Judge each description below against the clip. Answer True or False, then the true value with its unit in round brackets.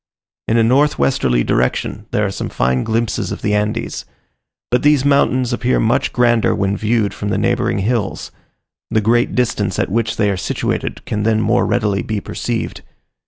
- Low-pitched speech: True (115 Hz)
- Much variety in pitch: False (2.8 semitones)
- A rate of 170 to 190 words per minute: True (175 wpm)